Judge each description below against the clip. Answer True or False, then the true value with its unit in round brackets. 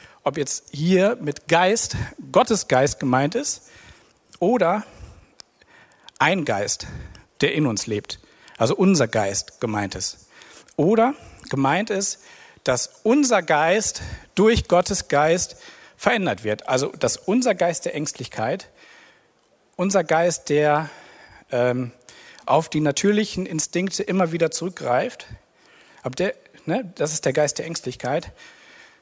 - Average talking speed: False (120 wpm)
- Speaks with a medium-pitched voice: True (160 Hz)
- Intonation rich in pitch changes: True (7.1 semitones)